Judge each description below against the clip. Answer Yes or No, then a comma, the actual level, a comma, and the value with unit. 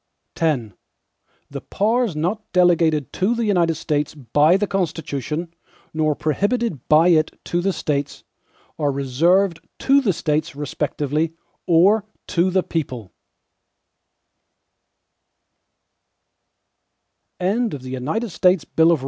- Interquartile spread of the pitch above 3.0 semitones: Yes, average, 4.1 semitones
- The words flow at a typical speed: No, slow, 90 wpm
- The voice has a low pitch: No, medium, 165 Hz